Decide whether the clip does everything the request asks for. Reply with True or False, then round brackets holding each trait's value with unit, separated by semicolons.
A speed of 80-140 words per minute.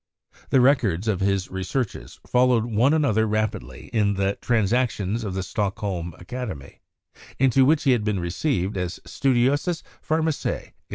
True (135 wpm)